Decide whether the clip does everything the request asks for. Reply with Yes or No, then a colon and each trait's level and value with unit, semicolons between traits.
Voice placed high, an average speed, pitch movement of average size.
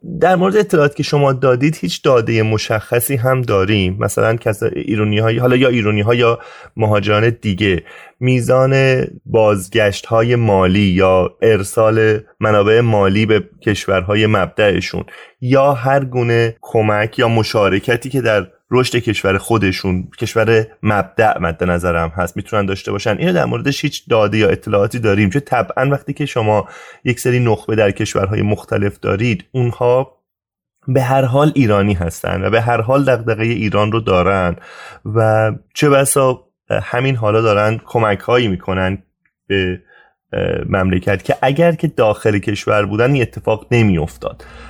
No: low, 110 Hz; average, 145 wpm; average, 4.0 semitones